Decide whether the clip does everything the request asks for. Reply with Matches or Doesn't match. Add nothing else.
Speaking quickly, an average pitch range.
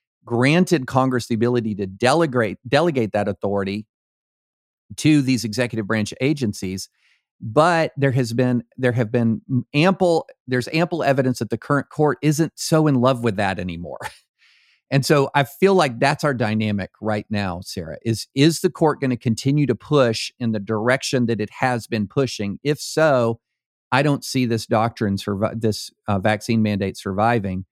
Doesn't match